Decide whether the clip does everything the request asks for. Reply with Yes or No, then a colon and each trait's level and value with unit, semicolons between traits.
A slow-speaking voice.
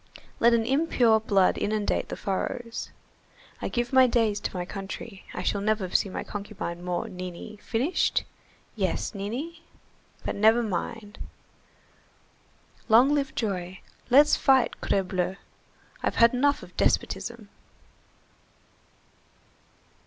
Yes: slow, 115 wpm